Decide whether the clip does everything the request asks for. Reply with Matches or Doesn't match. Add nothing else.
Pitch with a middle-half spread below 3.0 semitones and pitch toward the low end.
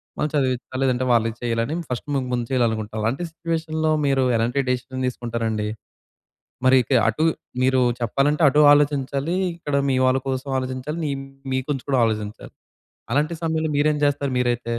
Doesn't match